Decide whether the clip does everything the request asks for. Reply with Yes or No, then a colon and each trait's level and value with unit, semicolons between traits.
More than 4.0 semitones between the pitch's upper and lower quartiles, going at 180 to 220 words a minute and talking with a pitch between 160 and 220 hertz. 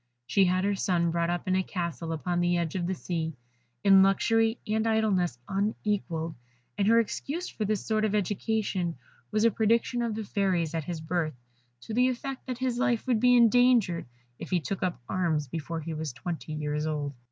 Yes: average, 4.7 semitones; average, 195 wpm; high, 190 Hz